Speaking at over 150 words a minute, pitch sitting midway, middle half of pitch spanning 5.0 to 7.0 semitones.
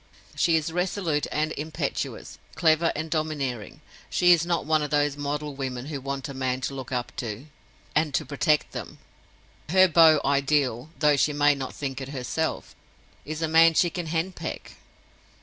No: average, 165 wpm; medium, 150 Hz; average, 2.8 semitones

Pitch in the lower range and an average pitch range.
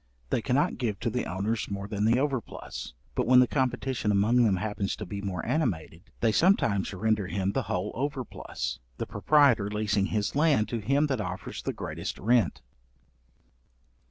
Yes: low, 110 Hz; average, 4.2 semitones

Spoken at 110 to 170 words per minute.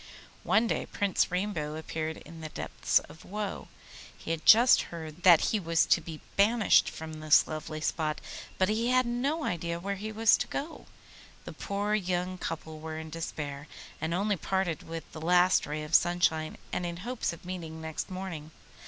No: average, 180 wpm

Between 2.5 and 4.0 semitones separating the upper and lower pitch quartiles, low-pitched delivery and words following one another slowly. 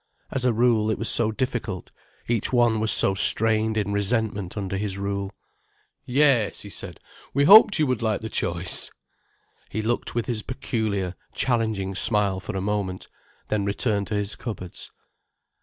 No: average, 2.9 semitones; low, 110 Hz; average, 160 wpm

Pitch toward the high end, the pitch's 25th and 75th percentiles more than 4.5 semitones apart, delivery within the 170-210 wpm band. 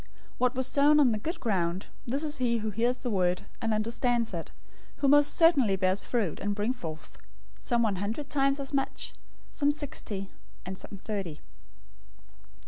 Yes: high, 230 Hz; wide, 5.6 semitones; average, 175 wpm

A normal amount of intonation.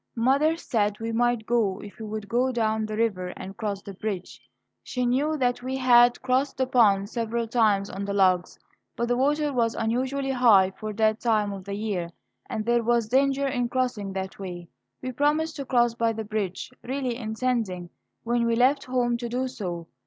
Yes: average, 3.5 semitones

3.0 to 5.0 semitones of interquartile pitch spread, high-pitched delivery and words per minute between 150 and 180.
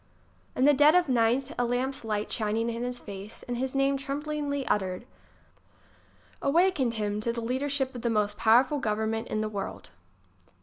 Yes: average, 3.9 semitones; high, 245 Hz; average, 175 wpm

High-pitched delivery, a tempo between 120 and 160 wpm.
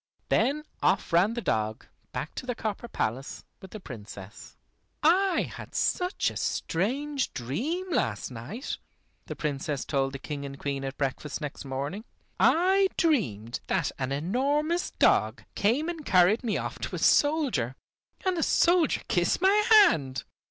Yes: high, 195 Hz; average, 150 wpm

